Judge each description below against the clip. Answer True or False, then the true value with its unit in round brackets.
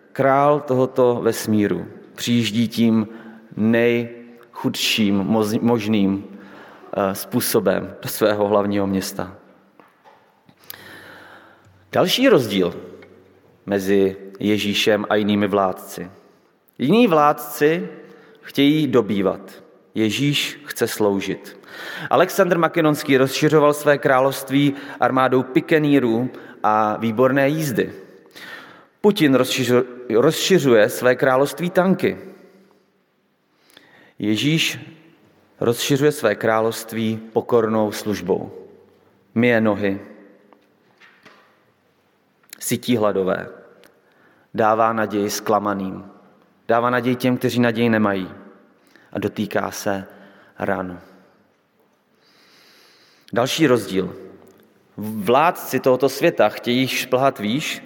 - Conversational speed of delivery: False (75 wpm)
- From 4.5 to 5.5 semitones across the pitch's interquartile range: True (4.9 semitones)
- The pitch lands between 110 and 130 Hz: True (115 Hz)